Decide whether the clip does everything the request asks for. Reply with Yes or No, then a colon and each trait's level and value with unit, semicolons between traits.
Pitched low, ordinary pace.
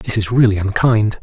Yes: low, 105 Hz; average, 195 wpm